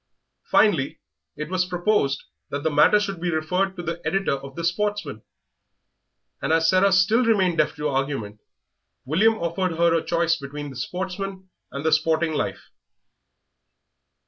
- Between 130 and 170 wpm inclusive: Yes, average, 145 wpm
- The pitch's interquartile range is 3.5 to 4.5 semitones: Yes, average, 4.1 semitones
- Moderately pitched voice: Yes, medium, 170 Hz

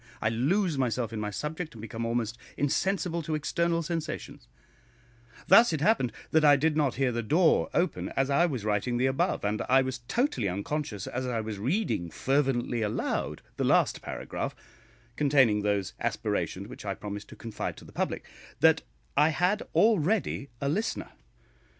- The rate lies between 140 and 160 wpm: No, average, 170 wpm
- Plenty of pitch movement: Yes, wide, 6.1 semitones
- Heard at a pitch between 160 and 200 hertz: No, low, 135 Hz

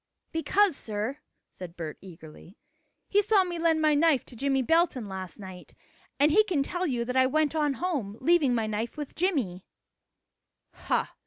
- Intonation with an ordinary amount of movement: No, wide, 7.5 semitones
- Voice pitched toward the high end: Yes, very high, 275 Hz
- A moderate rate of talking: Yes, average, 170 wpm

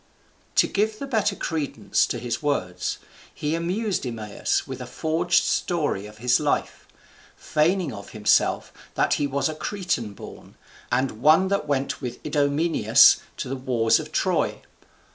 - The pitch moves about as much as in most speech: No, wide, 5.8 semitones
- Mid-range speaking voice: Yes, medium, 145 Hz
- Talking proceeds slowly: No, average, 150 wpm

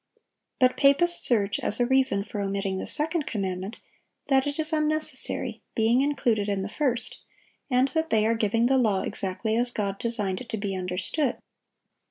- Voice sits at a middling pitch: No, high, 230 Hz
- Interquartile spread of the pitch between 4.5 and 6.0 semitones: Yes, average, 5.1 semitones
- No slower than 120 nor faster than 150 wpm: No, average, 175 wpm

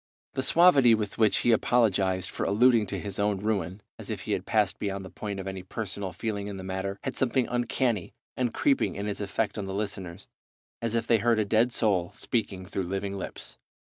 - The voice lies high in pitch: No, low, 105 Hz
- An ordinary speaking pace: No, fast, 210 wpm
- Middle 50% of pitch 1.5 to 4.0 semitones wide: Yes, average, 3.1 semitones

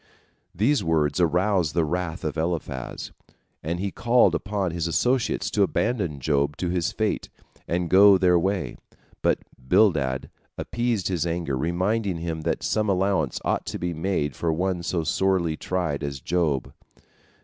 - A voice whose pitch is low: Yes, very low, 85 Hz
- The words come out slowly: No, average, 150 wpm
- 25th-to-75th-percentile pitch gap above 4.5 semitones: No, average, 3.4 semitones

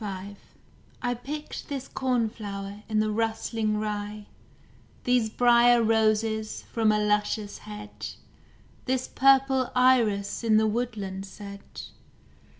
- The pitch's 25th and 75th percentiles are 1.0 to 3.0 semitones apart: Yes, narrow, 2.6 semitones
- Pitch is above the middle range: Yes, high, 220 Hz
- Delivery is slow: Yes, slow, 110 wpm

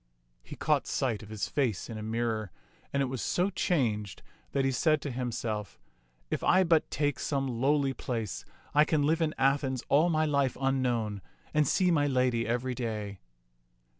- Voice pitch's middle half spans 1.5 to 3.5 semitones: No, average, 4.5 semitones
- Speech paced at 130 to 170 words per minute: No, average, 180 wpm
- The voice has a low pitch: Yes, low, 130 Hz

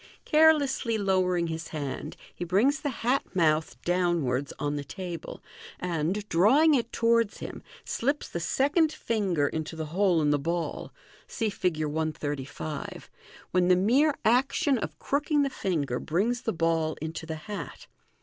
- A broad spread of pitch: Yes, wide, 6.8 semitones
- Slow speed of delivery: No, average, 145 wpm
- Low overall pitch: No, medium, 180 Hz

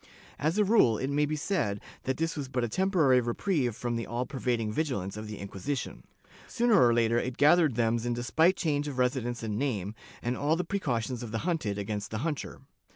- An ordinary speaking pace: No, fast, 210 wpm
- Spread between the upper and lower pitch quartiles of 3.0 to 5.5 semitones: Yes, average, 5.0 semitones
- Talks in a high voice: No, low, 125 Hz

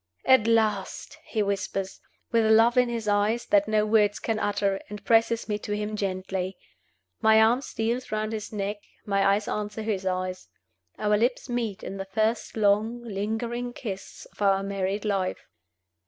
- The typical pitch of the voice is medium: No, high, 210 Hz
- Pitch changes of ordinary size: No, narrow, 2.3 semitones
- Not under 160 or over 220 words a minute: Yes, average, 165 wpm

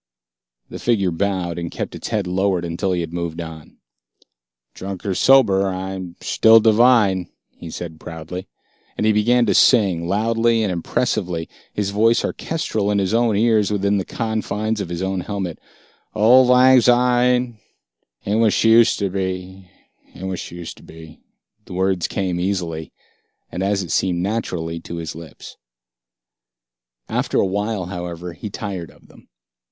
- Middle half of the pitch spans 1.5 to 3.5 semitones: No, average, 3.9 semitones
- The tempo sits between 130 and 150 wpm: No, average, 160 wpm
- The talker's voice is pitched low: Yes, very low, 95 Hz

